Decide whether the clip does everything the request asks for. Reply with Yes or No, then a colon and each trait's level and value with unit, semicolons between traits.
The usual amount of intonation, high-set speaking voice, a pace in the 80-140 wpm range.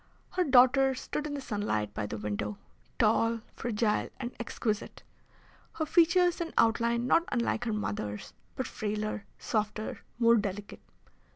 Yes: average, 4.1 semitones; high, 230 Hz; slow, 135 wpm